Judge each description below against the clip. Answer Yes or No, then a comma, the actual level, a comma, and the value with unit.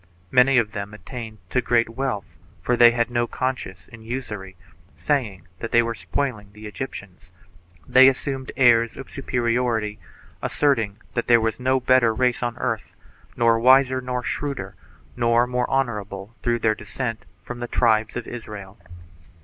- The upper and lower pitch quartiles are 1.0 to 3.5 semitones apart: Yes, average, 2.9 semitones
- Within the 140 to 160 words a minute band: Yes, average, 155 wpm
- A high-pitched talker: No, low, 120 Hz